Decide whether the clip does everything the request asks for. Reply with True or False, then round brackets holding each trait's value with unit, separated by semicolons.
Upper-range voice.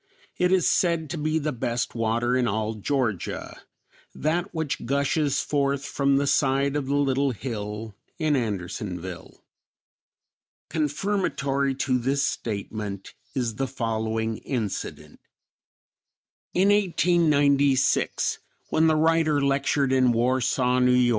False (135 Hz)